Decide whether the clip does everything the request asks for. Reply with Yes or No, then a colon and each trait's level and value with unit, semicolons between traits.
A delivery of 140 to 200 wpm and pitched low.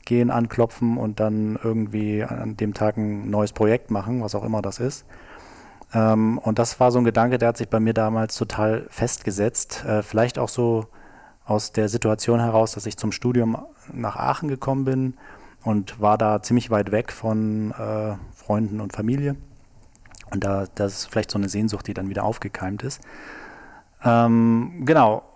Yes: average, 165 wpm; low, 110 Hz